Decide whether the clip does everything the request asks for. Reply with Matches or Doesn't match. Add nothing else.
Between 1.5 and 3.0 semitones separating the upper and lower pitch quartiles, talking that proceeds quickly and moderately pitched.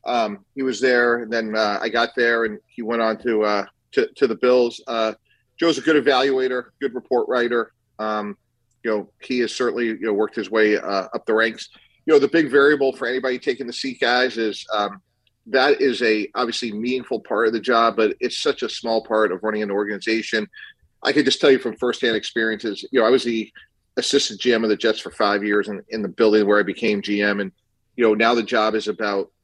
Doesn't match